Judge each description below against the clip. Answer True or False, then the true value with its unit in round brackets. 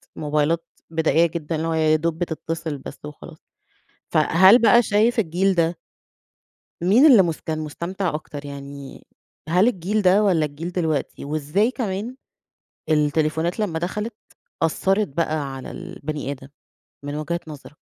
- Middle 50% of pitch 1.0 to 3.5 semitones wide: False (3.9 semitones)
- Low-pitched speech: False (165 Hz)